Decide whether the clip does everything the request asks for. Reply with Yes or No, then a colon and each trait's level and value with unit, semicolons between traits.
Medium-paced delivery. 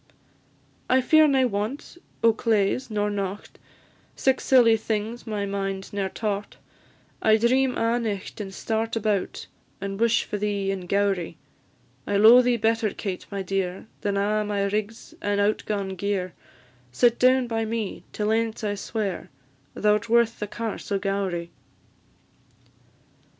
Yes: average, 150 wpm